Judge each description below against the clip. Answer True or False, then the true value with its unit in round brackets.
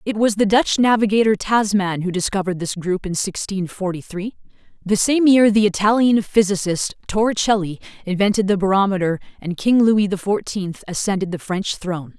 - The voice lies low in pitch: False (200 Hz)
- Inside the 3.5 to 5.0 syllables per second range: False (5.3 syllables/s)